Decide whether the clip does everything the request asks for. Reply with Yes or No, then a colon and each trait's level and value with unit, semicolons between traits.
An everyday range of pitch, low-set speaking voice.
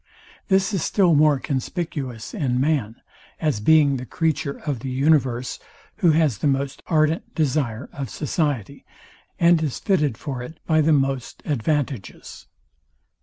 No: average, 3.5 semitones; medium, 145 Hz